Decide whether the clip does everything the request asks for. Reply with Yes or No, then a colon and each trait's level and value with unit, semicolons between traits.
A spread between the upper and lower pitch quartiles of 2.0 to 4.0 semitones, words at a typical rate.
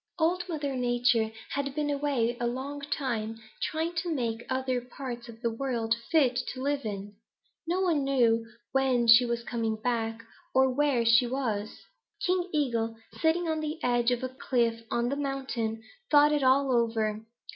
Yes: average, 3.6 semitones; average, 170 wpm